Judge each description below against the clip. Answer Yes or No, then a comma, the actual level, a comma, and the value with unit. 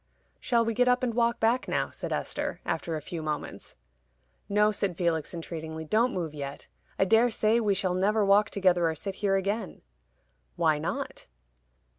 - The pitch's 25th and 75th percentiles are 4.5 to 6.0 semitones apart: Yes, average, 5.2 semitones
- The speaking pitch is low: No, high, 195 Hz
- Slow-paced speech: No, average, 175 wpm